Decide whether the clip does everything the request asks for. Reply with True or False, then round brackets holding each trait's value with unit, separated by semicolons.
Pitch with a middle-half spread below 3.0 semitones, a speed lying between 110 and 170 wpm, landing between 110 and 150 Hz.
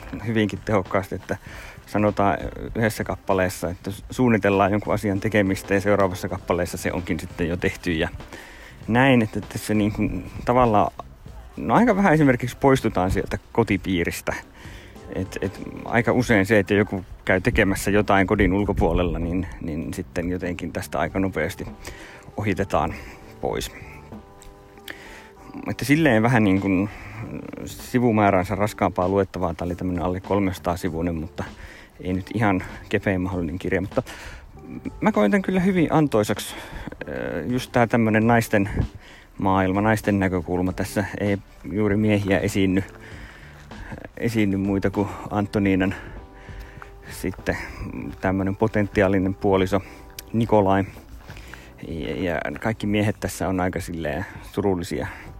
False (2.4 semitones; 120 wpm; 100 Hz)